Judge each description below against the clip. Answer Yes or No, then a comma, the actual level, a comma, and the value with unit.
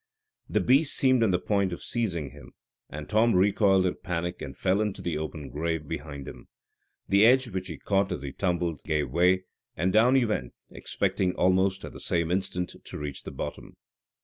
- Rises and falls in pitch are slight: No, average, 3.8 semitones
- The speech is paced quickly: No, average, 195 wpm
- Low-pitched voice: Yes, very low, 90 Hz